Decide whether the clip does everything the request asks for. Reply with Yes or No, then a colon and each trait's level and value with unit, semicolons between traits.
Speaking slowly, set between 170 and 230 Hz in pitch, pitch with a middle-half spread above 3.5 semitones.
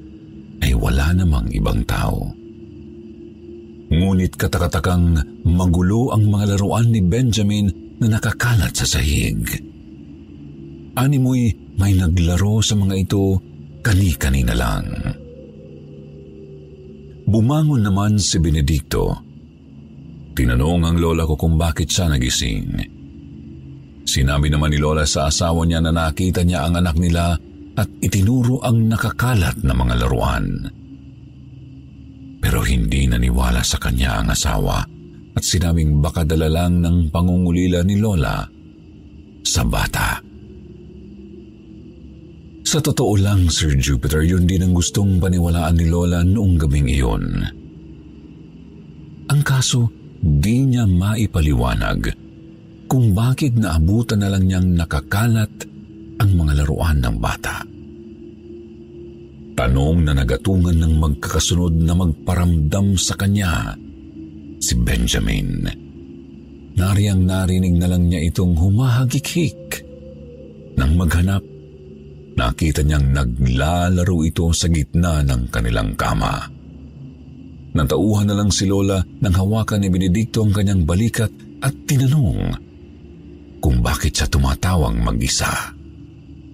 No: slow, 105 wpm; very low, 85 Hz; average, 5.3 semitones